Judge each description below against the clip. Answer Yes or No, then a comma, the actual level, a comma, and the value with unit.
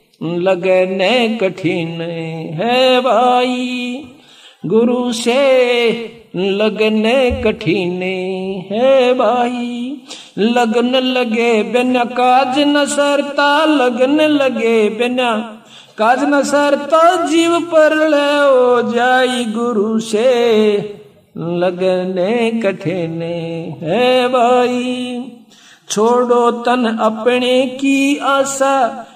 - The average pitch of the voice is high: Yes, high, 240 Hz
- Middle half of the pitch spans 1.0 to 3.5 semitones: Yes, average, 3.2 semitones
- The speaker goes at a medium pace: No, slow, 75 wpm